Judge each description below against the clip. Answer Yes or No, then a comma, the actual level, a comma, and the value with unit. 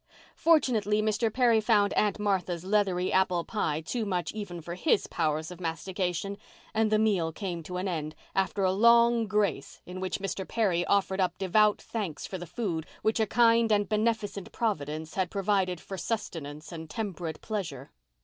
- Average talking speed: Yes, average, 170 wpm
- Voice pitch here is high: Yes, high, 195 Hz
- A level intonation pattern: No, average, 3.6 semitones